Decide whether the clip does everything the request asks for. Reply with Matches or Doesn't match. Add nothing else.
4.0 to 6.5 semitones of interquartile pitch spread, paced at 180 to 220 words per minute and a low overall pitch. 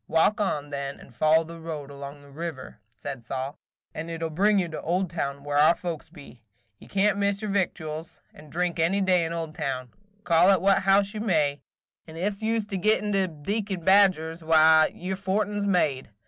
Doesn't match